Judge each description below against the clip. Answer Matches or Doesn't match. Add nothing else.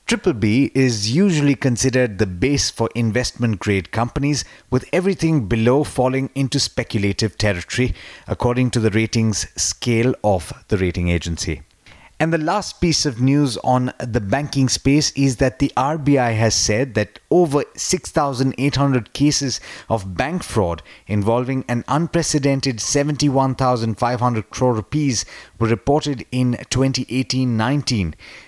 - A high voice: Doesn't match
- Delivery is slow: Matches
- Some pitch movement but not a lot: Matches